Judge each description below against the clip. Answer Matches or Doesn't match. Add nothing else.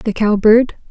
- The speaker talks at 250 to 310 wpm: Doesn't match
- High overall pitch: Matches